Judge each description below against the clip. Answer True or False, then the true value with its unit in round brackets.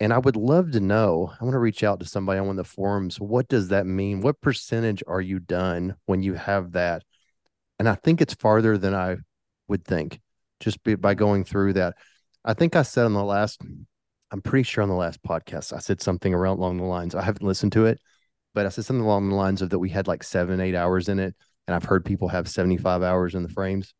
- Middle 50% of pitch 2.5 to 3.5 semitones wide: True (2.8 semitones)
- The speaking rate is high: True (245 wpm)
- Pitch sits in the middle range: False (100 Hz)